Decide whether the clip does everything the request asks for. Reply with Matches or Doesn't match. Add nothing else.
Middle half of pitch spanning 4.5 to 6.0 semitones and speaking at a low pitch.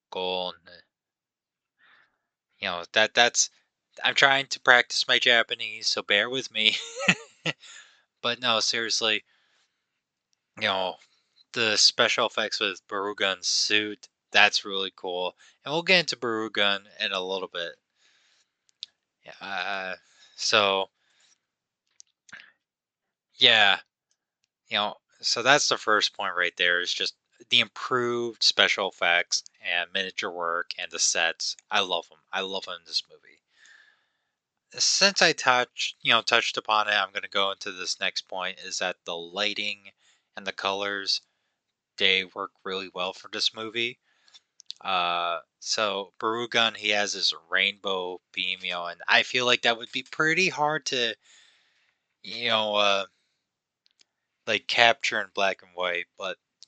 Matches